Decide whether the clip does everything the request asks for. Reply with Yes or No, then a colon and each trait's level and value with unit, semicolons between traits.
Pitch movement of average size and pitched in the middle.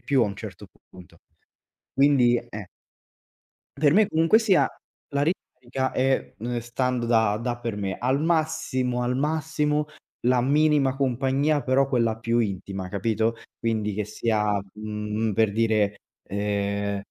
No: average, 4.5 semitones; low, 120 Hz